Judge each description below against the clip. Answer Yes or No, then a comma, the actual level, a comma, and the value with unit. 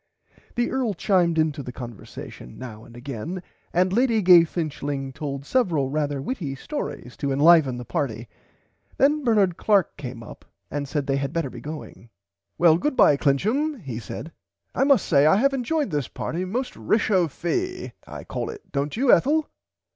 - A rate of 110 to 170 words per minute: Yes, average, 165 wpm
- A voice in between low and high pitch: Yes, medium, 165 Hz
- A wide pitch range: Yes, wide, 8.2 semitones